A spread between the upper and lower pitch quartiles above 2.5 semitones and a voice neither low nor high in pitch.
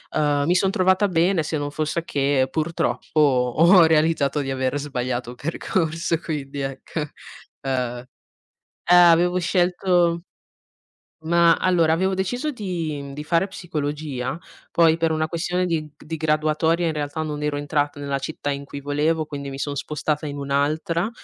Yes: average, 2.9 semitones; medium, 155 Hz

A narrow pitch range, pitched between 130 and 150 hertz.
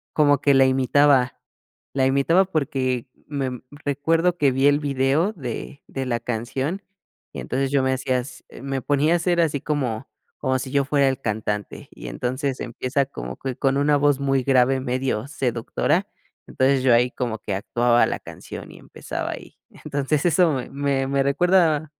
Yes: narrow, 2.1 semitones; low, 135 Hz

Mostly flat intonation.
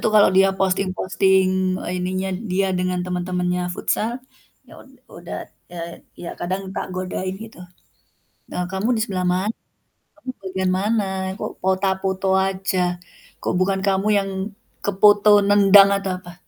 Yes: narrow, 1.3 semitones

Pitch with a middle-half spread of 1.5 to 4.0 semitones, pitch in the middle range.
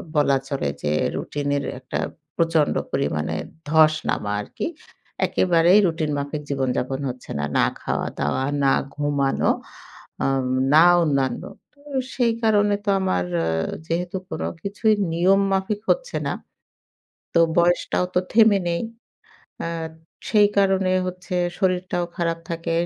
No: average, 5.3 semitones; medium, 165 Hz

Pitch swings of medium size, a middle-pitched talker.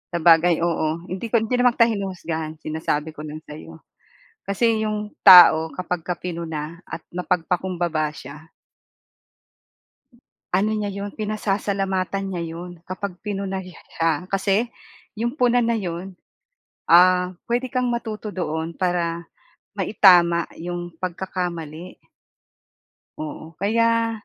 Yes: average, 3.7 semitones; medium, 180 Hz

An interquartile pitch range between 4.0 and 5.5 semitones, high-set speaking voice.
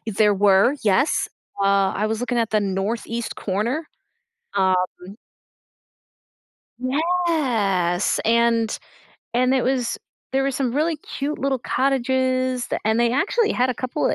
Yes: average, 4.3 semitones; high, 240 Hz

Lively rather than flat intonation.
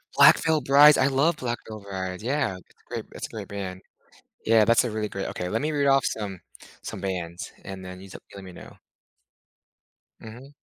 Yes: wide, 6.3 semitones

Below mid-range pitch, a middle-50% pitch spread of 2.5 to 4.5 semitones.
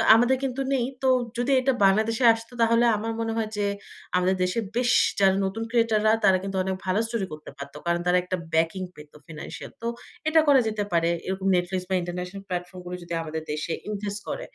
No: high, 195 Hz; average, 4.1 semitones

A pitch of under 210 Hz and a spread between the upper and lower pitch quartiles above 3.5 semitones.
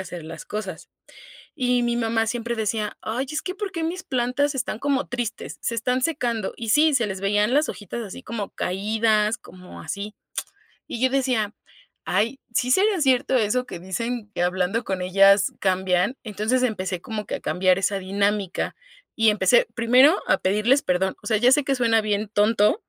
No: high, 225 Hz; average, 4.1 semitones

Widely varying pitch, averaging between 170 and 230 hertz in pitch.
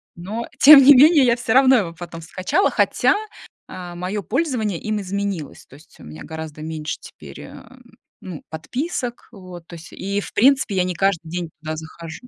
Yes: wide, 6.4 semitones; medium, 185 Hz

